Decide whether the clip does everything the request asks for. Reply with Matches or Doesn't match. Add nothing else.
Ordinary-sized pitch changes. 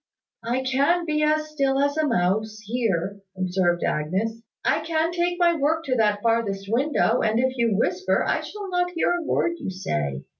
Doesn't match